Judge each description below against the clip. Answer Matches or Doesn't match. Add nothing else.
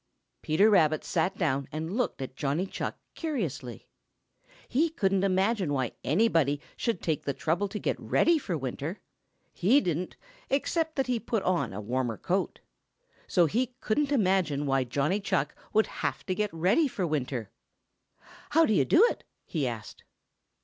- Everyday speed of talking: Matches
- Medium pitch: Matches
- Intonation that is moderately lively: Doesn't match